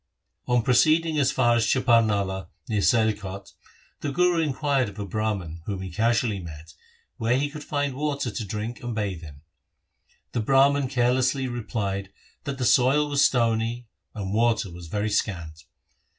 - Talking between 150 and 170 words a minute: Yes, average, 155 wpm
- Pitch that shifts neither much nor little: Yes, average, 4.9 semitones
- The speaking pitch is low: Yes, low, 115 Hz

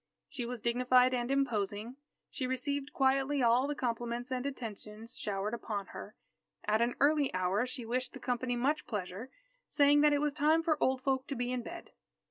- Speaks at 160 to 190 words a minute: Yes, average, 185 wpm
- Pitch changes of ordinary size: Yes, average, 3.0 semitones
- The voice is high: Yes, very high, 250 Hz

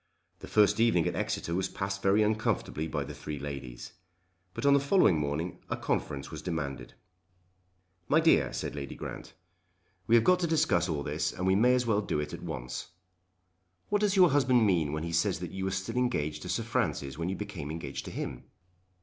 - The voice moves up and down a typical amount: No, wide, 7.2 semitones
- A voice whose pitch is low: Yes, very low, 95 Hz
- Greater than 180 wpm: Yes, fast, 205 wpm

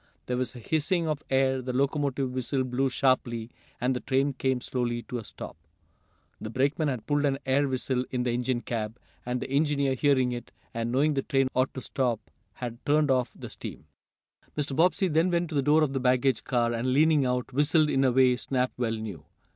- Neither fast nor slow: No, fast, 210 wpm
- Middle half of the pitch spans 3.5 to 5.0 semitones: No, narrow, 2.4 semitones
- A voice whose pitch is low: Yes, low, 130 Hz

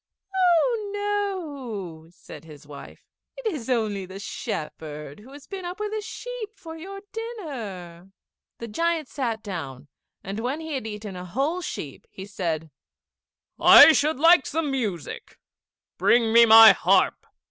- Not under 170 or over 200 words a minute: No, average, 145 wpm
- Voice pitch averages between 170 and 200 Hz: No, high, 245 Hz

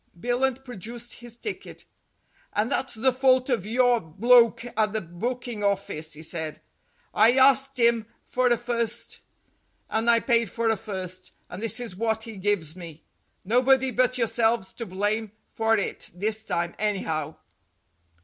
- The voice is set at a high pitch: Yes, high, 225 Hz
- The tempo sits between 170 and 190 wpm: No, average, 150 wpm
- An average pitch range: Yes, average, 3.6 semitones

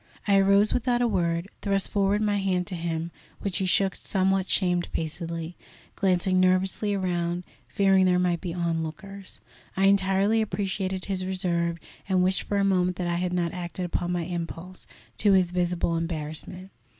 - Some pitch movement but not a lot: No, narrow, 2.1 semitones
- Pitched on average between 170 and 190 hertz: Yes, medium, 185 Hz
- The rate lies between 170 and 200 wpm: No, average, 160 wpm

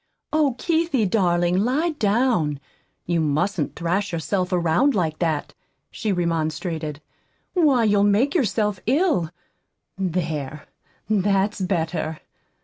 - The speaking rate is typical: No, slow, 105 wpm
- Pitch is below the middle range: No, medium, 185 Hz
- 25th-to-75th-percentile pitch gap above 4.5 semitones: Yes, wide, 5.6 semitones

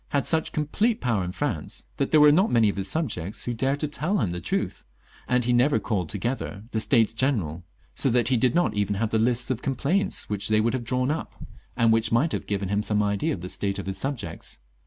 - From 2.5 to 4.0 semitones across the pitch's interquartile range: No, average, 5.1 semitones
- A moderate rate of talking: No, fast, 250 wpm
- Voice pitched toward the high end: No, low, 115 Hz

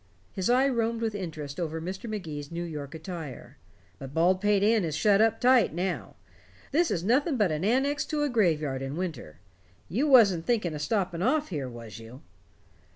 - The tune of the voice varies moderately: No, wide, 6.9 semitones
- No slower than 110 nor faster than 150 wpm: No, average, 180 wpm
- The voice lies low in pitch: No, medium, 185 Hz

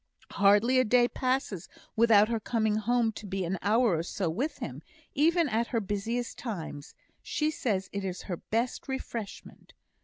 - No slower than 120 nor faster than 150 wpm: No, average, 165 wpm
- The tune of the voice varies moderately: Yes, average, 3.7 semitones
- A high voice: Yes, high, 220 Hz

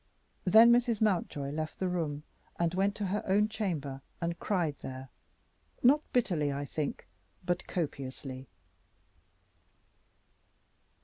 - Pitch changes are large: Yes, wide, 6.1 semitones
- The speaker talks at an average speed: No, slow, 115 wpm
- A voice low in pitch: No, medium, 170 Hz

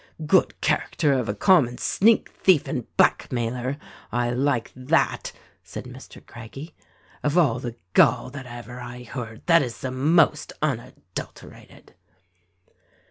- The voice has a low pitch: Yes, low, 125 Hz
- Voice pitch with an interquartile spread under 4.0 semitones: Yes, average, 3.3 semitones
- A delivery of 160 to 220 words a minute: No, slow, 135 wpm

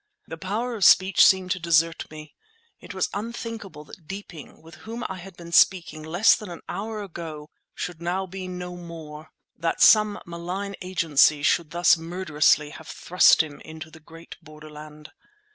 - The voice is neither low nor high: Yes, medium, 170 Hz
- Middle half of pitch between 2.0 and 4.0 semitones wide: Yes, average, 3.2 semitones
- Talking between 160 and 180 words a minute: Yes, average, 165 wpm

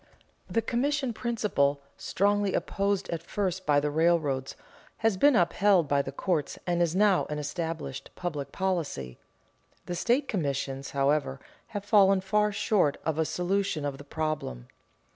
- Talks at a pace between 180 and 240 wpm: No, average, 145 wpm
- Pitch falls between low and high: Yes, medium, 175 Hz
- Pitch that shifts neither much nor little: No, wide, 5.8 semitones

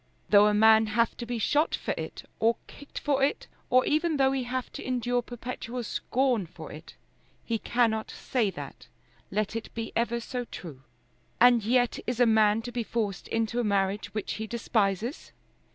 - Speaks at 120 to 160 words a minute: No, average, 185 wpm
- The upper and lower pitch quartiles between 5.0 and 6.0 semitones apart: No, narrow, 2.5 semitones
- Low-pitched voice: No, high, 230 Hz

